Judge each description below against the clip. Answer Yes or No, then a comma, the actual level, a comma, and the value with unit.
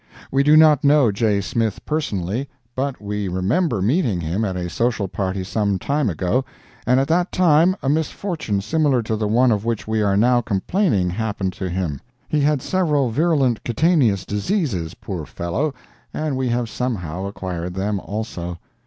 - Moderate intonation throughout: No, wide, 6.8 semitones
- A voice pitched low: Yes, low, 110 Hz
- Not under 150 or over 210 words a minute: Yes, average, 170 wpm